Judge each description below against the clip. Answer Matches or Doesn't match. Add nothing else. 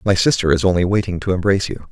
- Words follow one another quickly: Matches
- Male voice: Matches